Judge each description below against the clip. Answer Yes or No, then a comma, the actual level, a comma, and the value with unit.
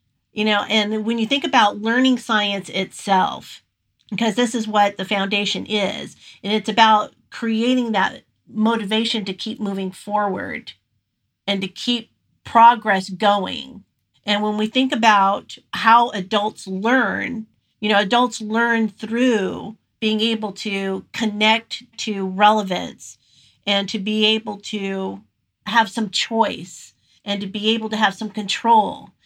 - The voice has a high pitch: Yes, high, 215 Hz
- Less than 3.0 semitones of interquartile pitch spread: Yes, narrow, 2.5 semitones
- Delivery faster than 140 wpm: No, slow, 135 wpm